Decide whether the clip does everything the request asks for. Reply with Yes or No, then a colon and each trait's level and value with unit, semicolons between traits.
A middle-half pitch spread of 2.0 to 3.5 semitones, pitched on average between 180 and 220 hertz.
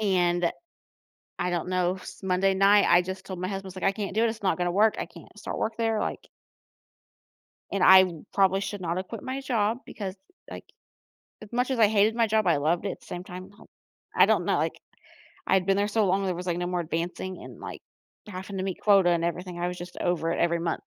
Yes: narrow, 2.6 semitones; high, 190 Hz